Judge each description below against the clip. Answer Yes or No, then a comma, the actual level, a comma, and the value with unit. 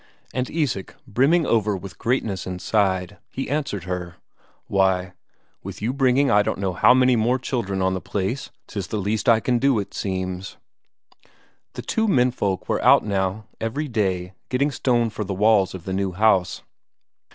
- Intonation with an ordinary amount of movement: Yes, average, 4.9 semitones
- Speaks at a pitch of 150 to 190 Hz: No, low, 105 Hz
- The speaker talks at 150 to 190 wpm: Yes, average, 170 wpm